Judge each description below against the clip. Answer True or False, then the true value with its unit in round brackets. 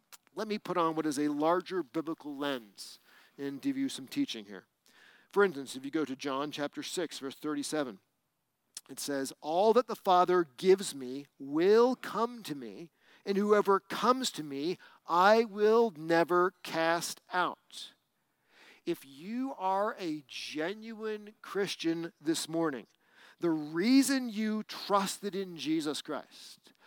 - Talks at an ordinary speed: True (145 wpm)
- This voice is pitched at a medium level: True (170 Hz)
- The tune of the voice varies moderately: False (6.4 semitones)